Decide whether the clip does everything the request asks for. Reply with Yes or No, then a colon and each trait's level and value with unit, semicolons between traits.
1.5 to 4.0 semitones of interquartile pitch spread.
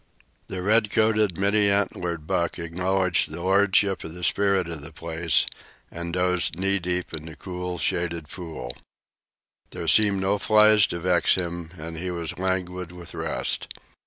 Yes: narrow, 2.6 semitones